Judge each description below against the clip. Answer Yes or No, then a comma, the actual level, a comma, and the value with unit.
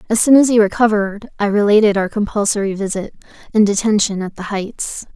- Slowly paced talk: No, average, 175 wpm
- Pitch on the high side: Yes, high, 205 Hz